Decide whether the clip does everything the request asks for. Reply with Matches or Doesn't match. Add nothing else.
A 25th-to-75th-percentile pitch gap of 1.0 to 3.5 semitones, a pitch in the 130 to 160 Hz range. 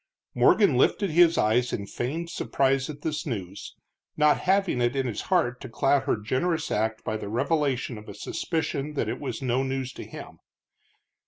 Doesn't match